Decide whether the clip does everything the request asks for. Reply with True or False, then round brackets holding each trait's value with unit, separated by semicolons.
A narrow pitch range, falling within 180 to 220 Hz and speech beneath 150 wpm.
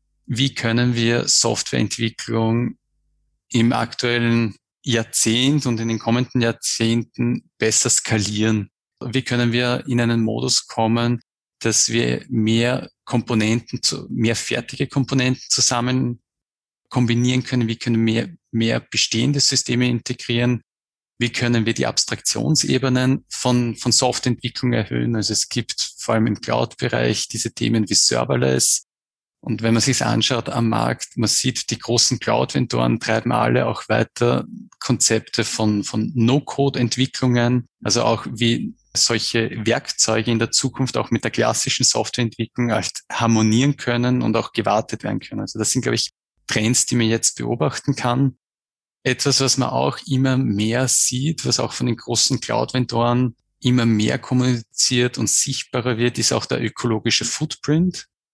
False (2.0 semitones; 120 Hz; 140 wpm)